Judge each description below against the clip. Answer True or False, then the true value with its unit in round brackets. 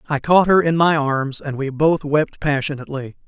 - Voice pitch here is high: False (145 Hz)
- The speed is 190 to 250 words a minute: True (200 wpm)